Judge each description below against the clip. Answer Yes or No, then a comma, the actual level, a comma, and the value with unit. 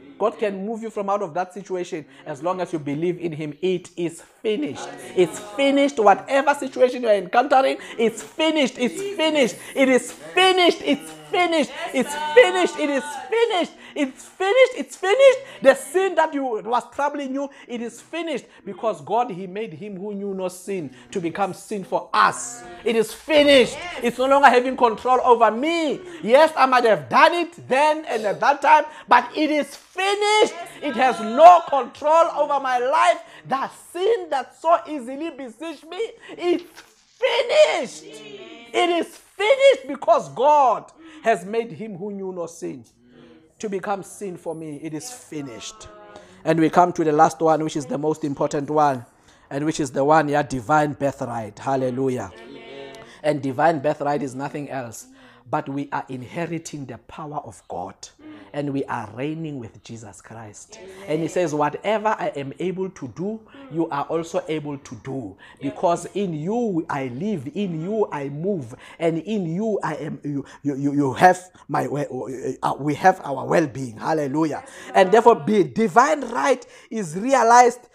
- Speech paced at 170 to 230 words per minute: Yes, average, 175 wpm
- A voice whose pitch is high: Yes, high, 210 Hz